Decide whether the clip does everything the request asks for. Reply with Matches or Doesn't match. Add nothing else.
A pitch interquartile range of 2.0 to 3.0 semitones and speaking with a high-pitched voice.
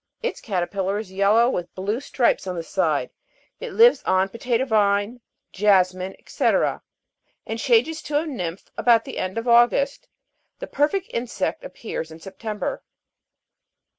Doesn't match